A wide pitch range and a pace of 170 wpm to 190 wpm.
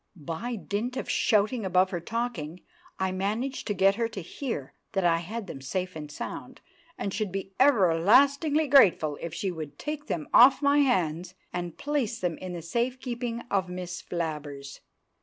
Yes: wide, 6.1 semitones; average, 175 wpm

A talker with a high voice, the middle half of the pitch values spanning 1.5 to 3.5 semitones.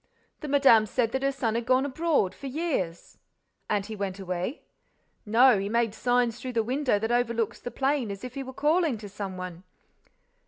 No: high, 235 Hz; average, 4.6 semitones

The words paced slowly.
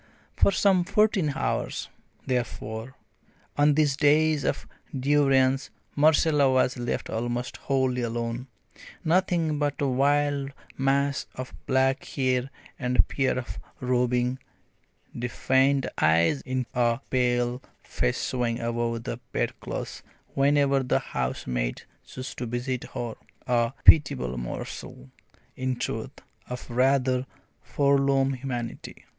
Yes: slow, 115 wpm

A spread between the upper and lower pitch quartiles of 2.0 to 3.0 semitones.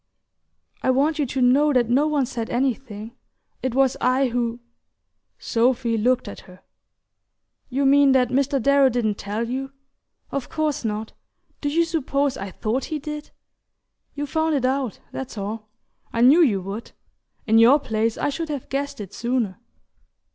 No: average, 3.6 semitones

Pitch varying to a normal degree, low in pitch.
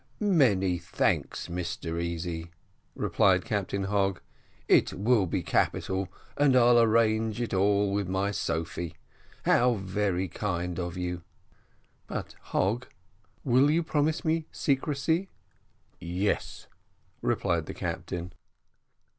No: wide, 5.7 semitones; low, 100 Hz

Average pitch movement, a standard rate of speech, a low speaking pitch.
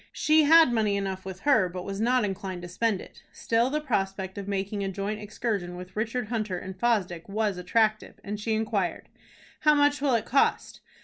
No: average, 3.6 semitones; average, 195 wpm; high, 210 Hz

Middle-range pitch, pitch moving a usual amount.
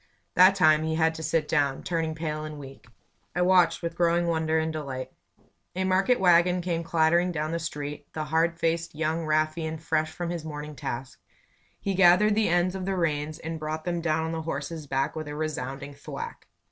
No: medium, 160 Hz; narrow, 2.0 semitones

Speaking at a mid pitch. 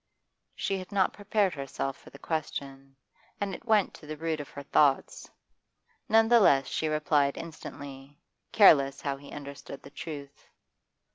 Yes: medium, 150 Hz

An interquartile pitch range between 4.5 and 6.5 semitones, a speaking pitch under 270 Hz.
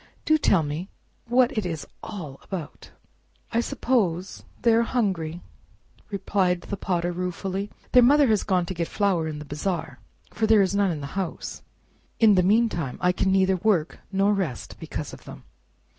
No: average, 3.9 semitones; high, 190 Hz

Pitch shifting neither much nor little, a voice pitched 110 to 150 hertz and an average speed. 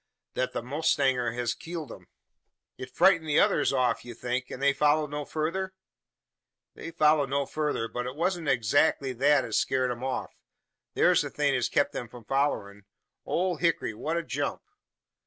Yes: average, 3.8 semitones; medium, 140 Hz; average, 175 wpm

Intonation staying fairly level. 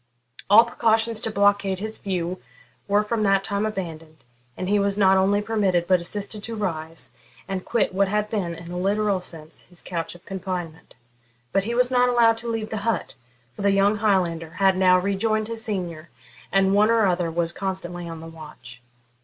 No: average, 3.3 semitones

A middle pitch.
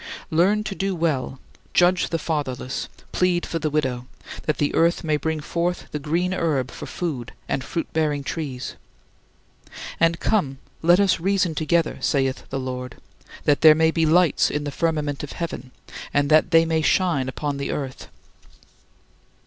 Yes: medium, 155 Hz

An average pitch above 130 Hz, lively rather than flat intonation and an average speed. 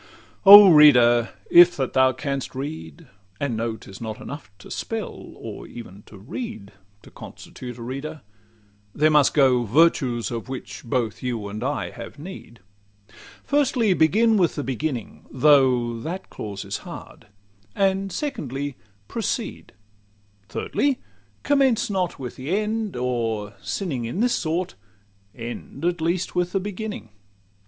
Yes: medium, 140 Hz; wide, 7.4 semitones; average, 145 wpm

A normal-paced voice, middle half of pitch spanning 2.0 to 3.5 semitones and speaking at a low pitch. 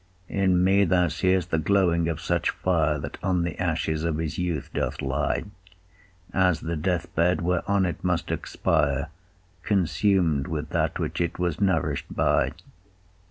Yes: average, 155 wpm; narrow, 2.6 semitones; very low, 85 Hz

